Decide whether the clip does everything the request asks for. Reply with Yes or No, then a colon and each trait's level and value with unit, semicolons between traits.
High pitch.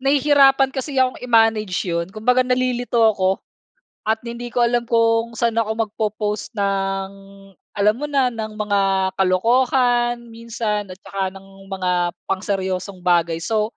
Yes: high, 220 Hz